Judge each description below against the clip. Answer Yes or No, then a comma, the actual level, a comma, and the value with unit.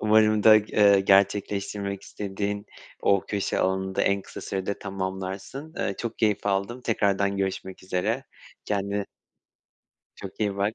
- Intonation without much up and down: Yes, narrow, 1.4 semitones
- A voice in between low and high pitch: No, low, 100 Hz